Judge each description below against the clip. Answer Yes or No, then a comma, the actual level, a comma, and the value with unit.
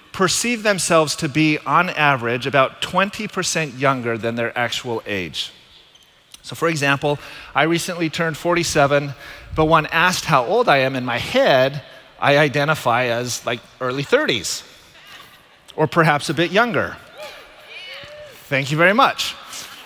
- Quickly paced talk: No, slow, 135 wpm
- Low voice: No, medium, 150 Hz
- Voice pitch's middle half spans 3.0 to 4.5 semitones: Yes, average, 4.2 semitones